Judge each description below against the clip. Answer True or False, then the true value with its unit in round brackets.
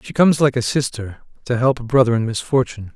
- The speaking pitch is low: True (125 Hz)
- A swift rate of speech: True (225 wpm)